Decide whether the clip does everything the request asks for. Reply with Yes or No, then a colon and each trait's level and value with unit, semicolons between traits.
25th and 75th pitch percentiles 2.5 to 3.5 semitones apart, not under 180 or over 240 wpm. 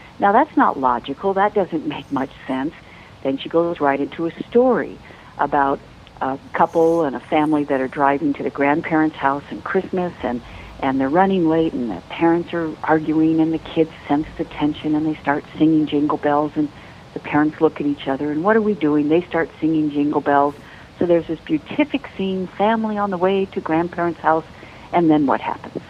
Yes: average, 2.9 semitones; average, 200 wpm